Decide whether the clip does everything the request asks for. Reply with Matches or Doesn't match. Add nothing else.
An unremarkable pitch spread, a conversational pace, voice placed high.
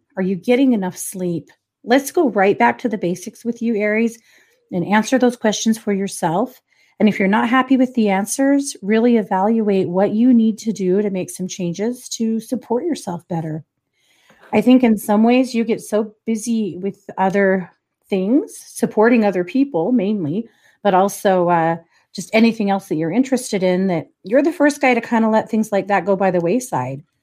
Matches